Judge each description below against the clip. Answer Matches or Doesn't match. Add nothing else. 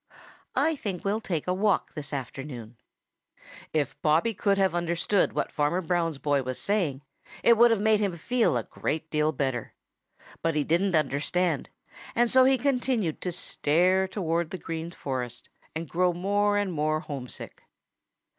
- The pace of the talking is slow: Doesn't match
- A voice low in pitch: Doesn't match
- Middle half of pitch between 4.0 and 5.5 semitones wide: Matches